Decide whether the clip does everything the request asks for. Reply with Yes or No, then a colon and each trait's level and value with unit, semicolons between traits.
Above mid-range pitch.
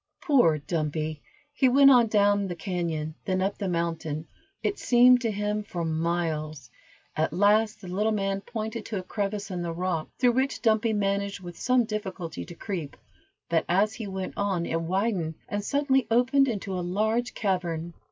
Yes: high, 195 Hz